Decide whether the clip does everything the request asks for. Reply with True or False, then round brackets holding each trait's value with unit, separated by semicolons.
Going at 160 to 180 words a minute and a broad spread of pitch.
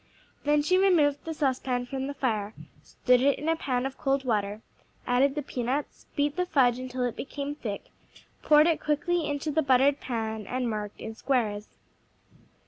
False (175 wpm; 3.2 semitones)